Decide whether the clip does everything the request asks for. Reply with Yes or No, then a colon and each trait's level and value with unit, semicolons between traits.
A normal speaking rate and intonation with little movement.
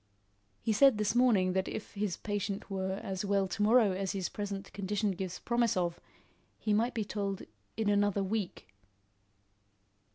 Yes: average, 160 wpm; narrow, 2.0 semitones